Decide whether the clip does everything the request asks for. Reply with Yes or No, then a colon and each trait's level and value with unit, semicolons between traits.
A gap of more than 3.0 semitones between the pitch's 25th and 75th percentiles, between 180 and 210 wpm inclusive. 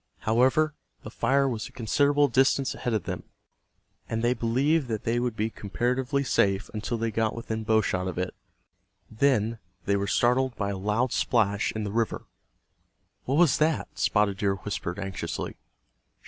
No: average, 3.9 semitones; average, 165 wpm